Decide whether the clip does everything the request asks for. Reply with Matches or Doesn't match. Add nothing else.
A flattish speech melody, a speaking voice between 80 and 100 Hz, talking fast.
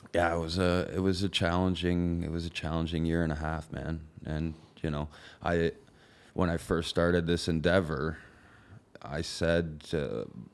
Doesn't match